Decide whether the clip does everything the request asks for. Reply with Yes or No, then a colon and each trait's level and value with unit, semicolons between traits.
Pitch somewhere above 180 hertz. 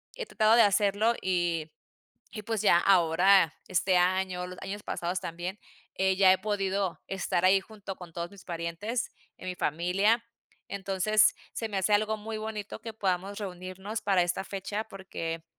Yes: high, 190 Hz